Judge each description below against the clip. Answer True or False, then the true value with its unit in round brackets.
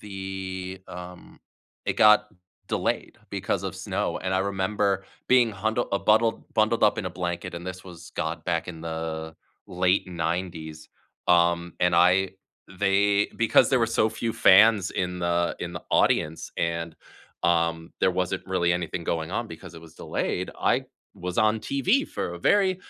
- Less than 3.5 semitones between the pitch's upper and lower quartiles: True (3.0 semitones)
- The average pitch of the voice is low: True (90 Hz)